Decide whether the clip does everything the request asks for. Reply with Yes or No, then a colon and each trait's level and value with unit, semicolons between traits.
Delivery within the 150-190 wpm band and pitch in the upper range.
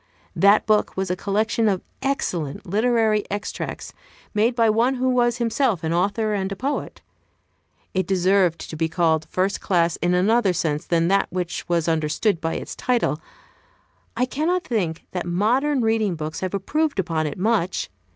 Yes: average, 165 wpm; high, 195 Hz